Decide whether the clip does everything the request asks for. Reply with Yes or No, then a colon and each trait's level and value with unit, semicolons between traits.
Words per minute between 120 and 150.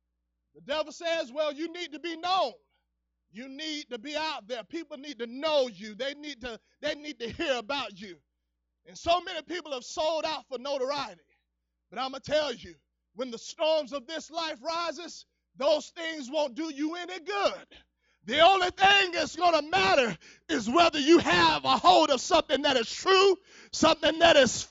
No: average, 195 wpm